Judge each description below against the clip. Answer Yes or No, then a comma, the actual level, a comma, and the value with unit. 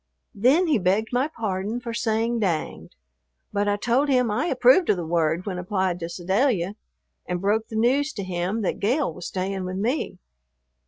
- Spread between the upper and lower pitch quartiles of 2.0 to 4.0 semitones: No, average, 4.9 semitones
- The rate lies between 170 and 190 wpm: Yes, average, 180 wpm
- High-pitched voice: Yes, high, 210 Hz